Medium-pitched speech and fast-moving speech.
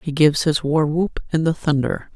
Yes: medium, 155 Hz; fast, 220 wpm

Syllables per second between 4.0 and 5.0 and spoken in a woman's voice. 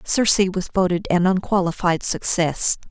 Yes: 4.7 syllables/s; female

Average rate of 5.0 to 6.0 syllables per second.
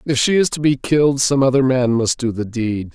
Yes: 5.4 syllables/s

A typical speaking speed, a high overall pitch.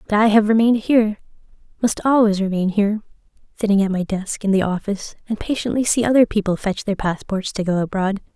Yes: average, 185 wpm; high, 205 Hz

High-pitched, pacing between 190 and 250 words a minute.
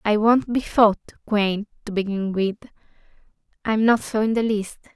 No: high, 215 Hz; average, 170 wpm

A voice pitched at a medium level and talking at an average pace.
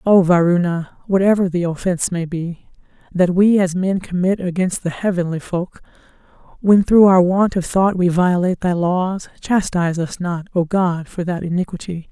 Yes: medium, 180 Hz; average, 170 wpm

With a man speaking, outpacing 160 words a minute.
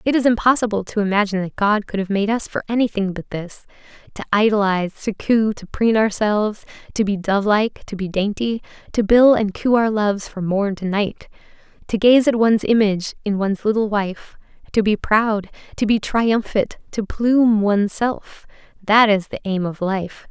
No: female; average, 185 wpm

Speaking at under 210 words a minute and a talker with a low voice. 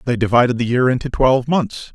No: fast, 215 wpm; low, 125 Hz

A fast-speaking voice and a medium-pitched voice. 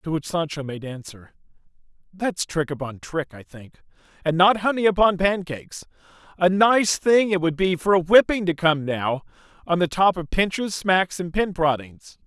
No: average, 180 wpm; medium, 170 Hz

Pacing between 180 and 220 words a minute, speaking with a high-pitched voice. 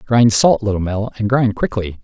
No: fast, 205 wpm; low, 110 Hz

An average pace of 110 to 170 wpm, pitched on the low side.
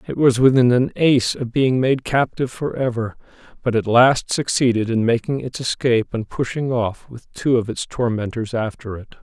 No: average, 190 wpm; low, 120 Hz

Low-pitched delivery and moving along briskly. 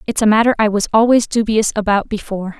No: high, 215 Hz; fast, 210 wpm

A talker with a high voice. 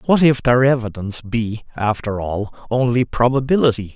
No: low, 120 Hz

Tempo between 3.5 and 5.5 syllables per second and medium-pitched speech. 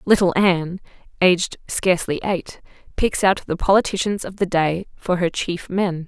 Yes: 4.8 syllables/s; medium, 180 Hz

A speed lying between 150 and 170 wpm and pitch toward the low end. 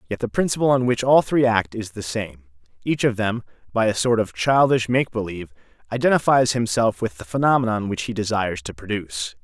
No: average, 195 wpm; low, 110 Hz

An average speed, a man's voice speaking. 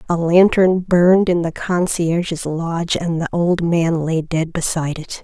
No: average, 170 wpm; female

